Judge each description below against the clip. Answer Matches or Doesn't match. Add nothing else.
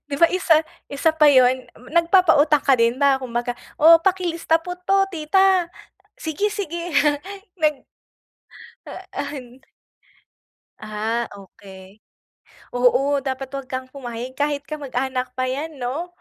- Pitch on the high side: Matches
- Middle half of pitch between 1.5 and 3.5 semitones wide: Doesn't match